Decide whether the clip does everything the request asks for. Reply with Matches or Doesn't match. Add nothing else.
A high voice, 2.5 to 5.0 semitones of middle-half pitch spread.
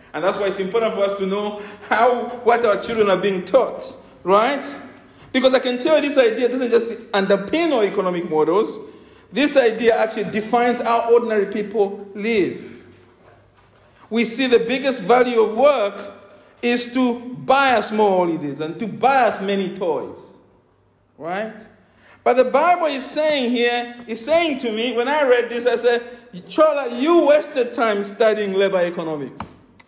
Matches